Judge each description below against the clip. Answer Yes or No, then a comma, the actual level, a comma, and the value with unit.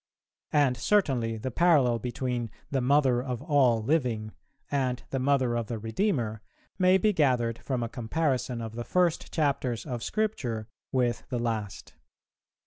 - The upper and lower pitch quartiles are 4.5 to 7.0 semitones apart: No, average, 3.6 semitones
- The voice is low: Yes, low, 125 Hz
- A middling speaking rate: Yes, average, 145 wpm